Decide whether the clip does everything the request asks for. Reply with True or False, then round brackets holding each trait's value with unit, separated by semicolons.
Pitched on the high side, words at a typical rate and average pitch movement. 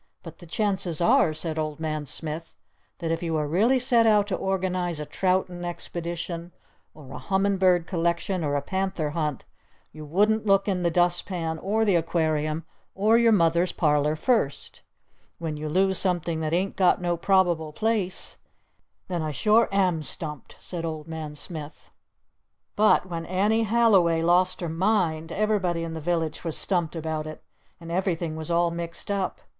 False (170 Hz; 170 wpm; 3.1 semitones)